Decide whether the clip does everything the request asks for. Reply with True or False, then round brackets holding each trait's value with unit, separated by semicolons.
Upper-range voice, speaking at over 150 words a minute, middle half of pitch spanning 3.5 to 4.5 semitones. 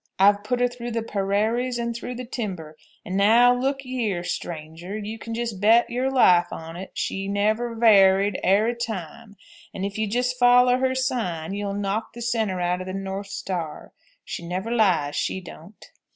True (210 Hz; 180 wpm; 4.0 semitones)